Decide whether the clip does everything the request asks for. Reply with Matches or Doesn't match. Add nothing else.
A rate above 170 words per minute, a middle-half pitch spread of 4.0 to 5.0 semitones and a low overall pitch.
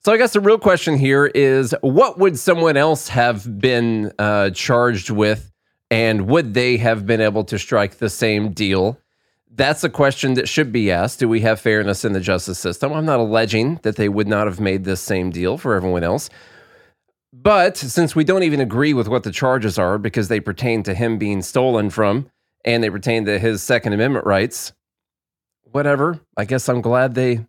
Matches